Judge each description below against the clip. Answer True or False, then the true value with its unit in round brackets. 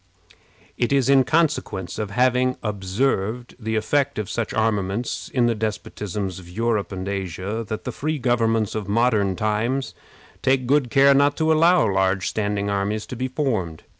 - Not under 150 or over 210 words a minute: True (165 wpm)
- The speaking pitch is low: True (110 Hz)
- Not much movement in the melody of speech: False (4.3 semitones)